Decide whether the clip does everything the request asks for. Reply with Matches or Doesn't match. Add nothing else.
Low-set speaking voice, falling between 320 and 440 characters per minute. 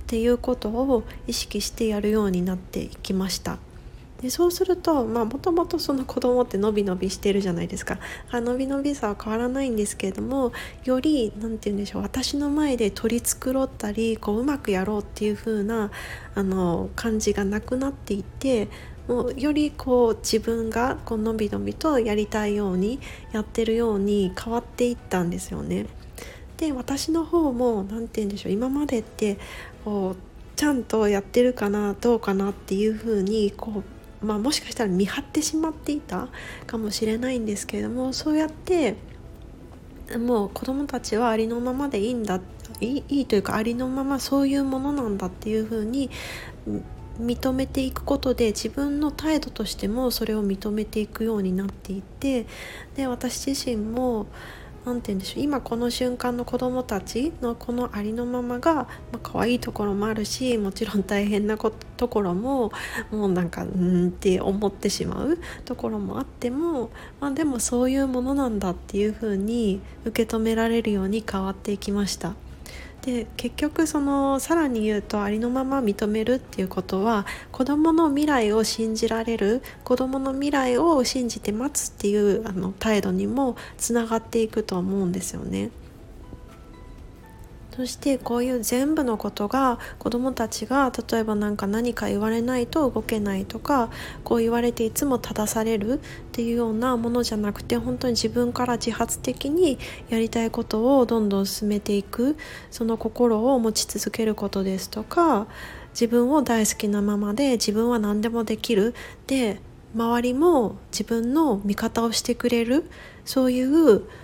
Doesn't match